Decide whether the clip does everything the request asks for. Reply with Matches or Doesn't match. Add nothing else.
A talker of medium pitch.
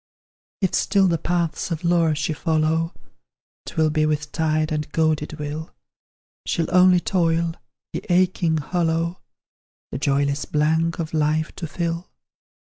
Matches